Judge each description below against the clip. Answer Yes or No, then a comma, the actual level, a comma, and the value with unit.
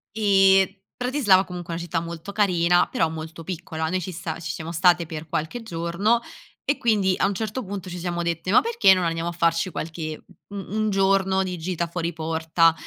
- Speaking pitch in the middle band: Yes, medium, 175 Hz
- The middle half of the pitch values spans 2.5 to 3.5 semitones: Yes, average, 2.8 semitones